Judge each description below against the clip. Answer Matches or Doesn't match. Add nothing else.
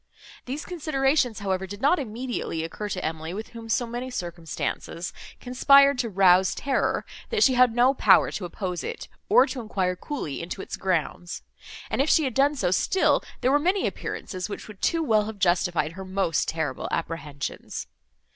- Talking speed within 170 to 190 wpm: Matches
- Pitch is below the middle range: Doesn't match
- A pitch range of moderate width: Doesn't match